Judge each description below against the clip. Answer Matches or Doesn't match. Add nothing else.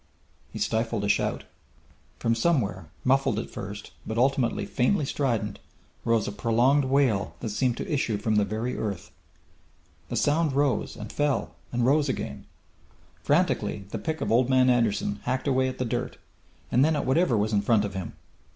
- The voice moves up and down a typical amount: Matches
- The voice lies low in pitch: Matches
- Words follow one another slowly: Doesn't match